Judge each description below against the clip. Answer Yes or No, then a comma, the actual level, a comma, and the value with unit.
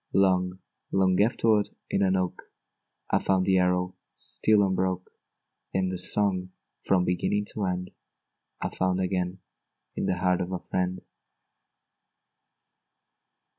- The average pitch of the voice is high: No, very low, 95 Hz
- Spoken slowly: Yes, slow, 125 wpm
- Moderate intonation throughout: No, narrow, 1.0 semitones